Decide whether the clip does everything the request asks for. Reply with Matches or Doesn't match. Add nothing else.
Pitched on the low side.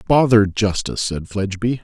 Matches